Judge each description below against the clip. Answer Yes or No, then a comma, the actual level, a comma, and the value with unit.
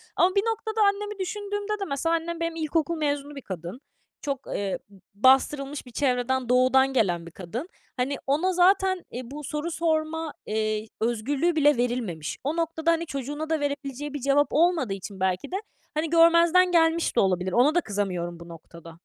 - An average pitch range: No, wide, 6.0 semitones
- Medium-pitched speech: No, very high, 290 Hz